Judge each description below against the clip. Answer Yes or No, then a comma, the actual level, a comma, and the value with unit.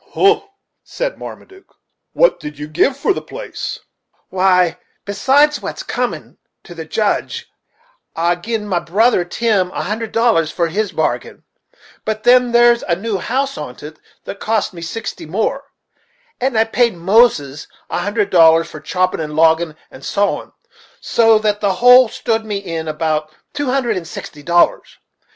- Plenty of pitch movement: Yes, wide, 5.9 semitones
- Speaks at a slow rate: No, average, 160 wpm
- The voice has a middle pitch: No, high, 200 Hz